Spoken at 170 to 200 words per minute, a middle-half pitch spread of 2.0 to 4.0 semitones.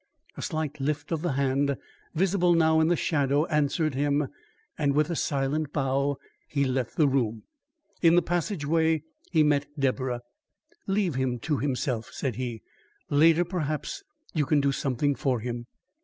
No: average, 155 wpm; average, 2.9 semitones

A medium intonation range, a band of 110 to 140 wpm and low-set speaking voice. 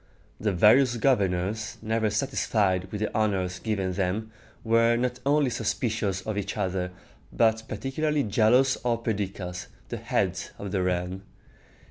Yes: average, 3.5 semitones; slow, 135 wpm; low, 110 Hz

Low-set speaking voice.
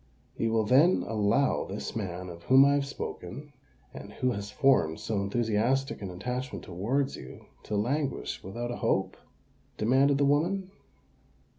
Yes: low, 120 Hz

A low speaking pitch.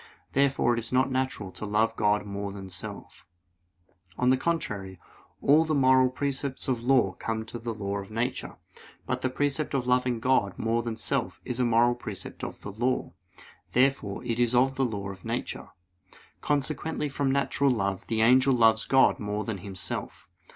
Yes: low, 120 Hz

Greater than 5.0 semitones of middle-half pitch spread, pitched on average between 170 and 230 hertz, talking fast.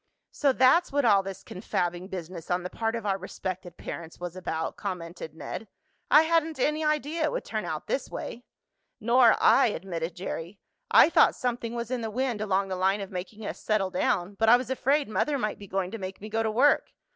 Yes: wide, 5.5 semitones; high, 210 Hz; fast, 215 wpm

